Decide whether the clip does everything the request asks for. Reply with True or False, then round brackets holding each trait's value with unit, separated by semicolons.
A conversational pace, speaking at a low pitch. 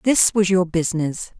False (170 wpm; 185 Hz)